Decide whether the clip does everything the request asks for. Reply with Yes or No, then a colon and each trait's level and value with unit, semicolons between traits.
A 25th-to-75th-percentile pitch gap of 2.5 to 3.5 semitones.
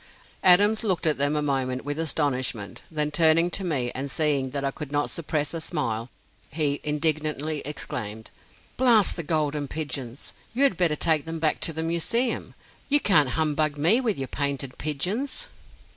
Yes: average, 2.9 semitones